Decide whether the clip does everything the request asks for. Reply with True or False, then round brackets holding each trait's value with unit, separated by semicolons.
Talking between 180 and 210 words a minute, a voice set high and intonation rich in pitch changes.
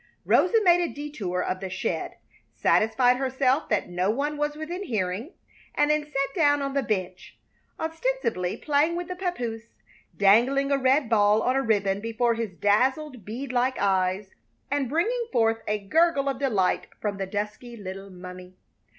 False (165 wpm; 245 Hz; 6.3 semitones)